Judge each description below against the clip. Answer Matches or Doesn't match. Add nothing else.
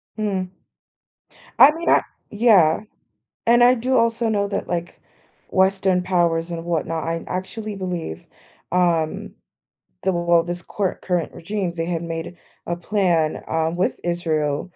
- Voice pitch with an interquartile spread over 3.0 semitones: Matches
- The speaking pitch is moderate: Matches